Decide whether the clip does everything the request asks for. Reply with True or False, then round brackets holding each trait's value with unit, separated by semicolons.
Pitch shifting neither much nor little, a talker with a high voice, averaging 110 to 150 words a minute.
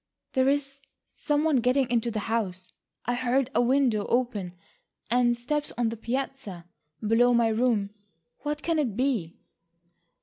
True (3.3 semitones; 245 Hz; 145 wpm)